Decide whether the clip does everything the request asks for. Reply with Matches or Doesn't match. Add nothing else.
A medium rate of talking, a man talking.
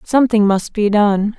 Doesn't match